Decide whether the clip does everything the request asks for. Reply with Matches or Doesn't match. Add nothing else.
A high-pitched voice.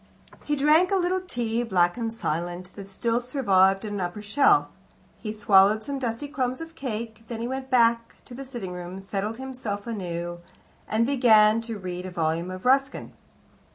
Matches